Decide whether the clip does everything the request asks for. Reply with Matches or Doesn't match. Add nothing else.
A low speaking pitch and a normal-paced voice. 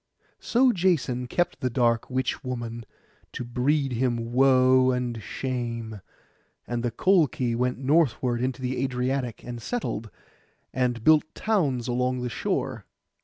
Doesn't match